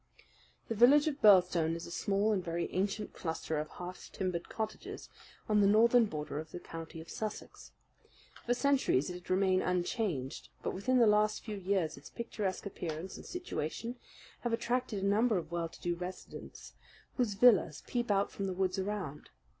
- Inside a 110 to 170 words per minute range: No, average, 180 wpm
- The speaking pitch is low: No, high, 195 Hz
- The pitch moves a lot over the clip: No, average, 4.2 semitones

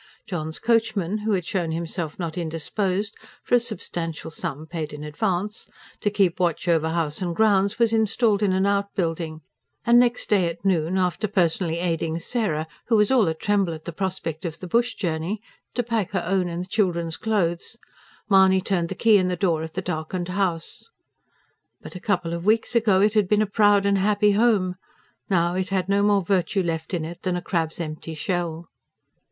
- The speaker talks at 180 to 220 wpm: Yes, average, 195 wpm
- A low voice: No, medium, 185 Hz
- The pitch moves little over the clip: No, average, 3.6 semitones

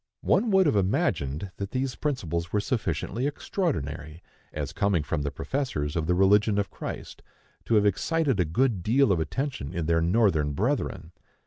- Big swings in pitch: Yes, wide, 8.0 semitones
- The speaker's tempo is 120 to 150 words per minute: No, average, 165 wpm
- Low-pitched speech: Yes, low, 100 Hz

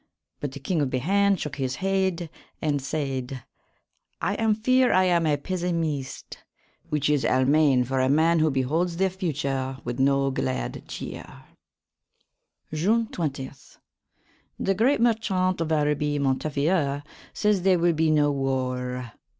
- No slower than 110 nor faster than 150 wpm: Yes, average, 140 wpm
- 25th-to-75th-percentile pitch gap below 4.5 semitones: No, average, 5.3 semitones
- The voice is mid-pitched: Yes, medium, 150 Hz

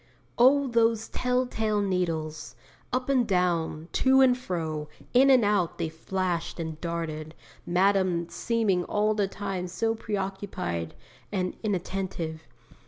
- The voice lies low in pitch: No, high, 190 Hz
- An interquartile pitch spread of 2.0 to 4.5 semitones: No, average, 5.0 semitones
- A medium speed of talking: No, slow, 130 wpm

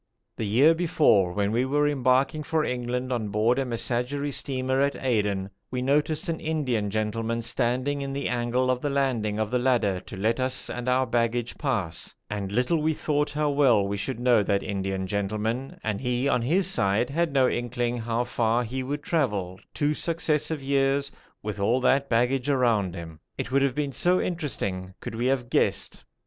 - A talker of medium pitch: No, low, 125 Hz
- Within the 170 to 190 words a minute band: Yes, average, 185 wpm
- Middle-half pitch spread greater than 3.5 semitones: Yes, average, 4.2 semitones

